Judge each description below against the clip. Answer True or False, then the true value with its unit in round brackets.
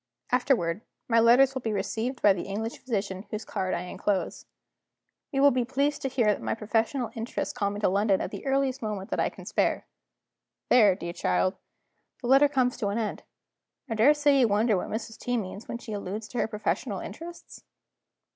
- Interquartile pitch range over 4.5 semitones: False (4.0 semitones)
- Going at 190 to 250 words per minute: True (195 wpm)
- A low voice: False (225 Hz)